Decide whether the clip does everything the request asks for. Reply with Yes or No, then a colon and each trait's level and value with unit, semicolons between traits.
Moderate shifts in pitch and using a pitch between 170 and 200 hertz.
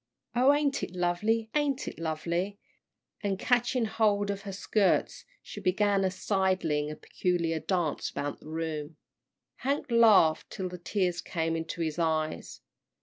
Yes: average, 4.6 semitones; medium, 185 Hz